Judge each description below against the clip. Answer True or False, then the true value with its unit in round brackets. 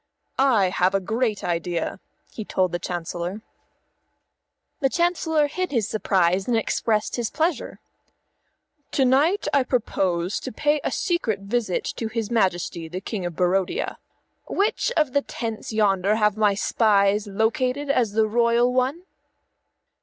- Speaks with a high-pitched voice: True (220 Hz)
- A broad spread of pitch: False (5.0 semitones)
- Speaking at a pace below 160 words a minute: True (145 wpm)